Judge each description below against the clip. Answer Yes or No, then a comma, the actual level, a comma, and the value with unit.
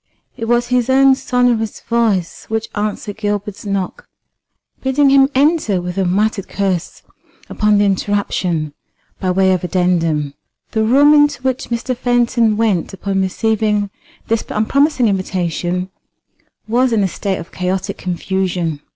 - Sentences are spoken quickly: No, slow, 135 wpm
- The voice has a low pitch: No, high, 205 Hz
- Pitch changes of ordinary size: Yes, average, 4.4 semitones